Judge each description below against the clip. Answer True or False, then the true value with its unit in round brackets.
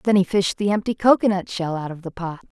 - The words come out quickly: True (265 wpm)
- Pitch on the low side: False (190 Hz)